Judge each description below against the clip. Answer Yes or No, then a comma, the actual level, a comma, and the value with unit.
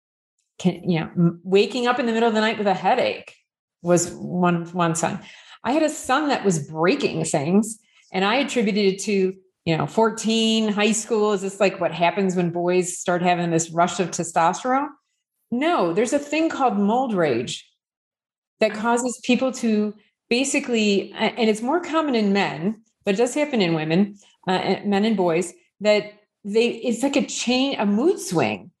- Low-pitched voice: No, high, 210 Hz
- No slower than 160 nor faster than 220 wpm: Yes, average, 180 wpm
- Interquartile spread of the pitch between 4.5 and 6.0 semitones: Yes, average, 5.0 semitones